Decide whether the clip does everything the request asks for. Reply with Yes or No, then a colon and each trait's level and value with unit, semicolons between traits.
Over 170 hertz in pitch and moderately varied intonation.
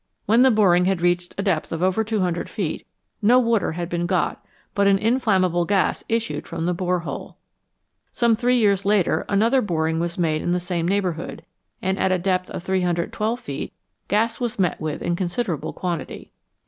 Yes: medium, 185 Hz; average, 3.7 semitones